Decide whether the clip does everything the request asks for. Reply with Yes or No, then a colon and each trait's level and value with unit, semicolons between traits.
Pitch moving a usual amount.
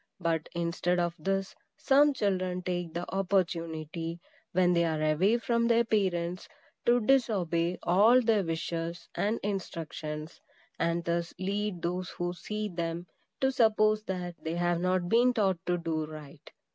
Yes: average, 3.6 semitones